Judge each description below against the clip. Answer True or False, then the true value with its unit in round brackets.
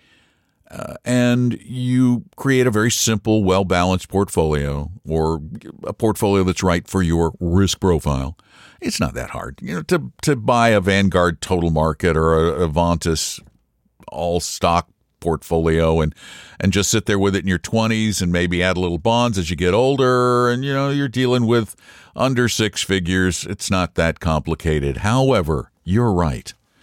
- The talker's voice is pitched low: True (95 Hz)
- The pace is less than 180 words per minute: True (165 wpm)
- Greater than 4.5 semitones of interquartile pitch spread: True (5.4 semitones)